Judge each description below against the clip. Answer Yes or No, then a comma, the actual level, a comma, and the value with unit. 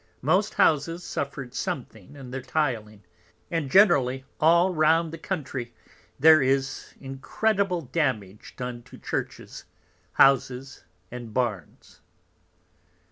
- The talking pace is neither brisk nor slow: No, slow, 105 wpm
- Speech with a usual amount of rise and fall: Yes, average, 4.6 semitones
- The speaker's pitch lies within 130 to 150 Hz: Yes, low, 135 Hz